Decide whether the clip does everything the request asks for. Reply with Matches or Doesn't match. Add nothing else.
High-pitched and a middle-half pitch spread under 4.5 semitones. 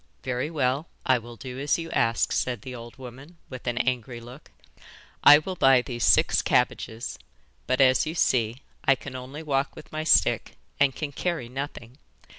Doesn't match